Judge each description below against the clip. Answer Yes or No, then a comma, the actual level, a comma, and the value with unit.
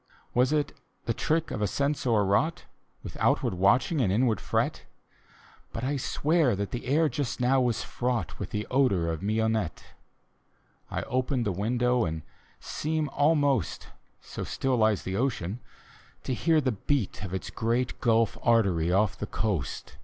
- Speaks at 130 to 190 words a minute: Yes, average, 170 wpm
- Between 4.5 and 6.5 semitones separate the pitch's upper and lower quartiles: Yes, average, 5.0 semitones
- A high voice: No, low, 120 Hz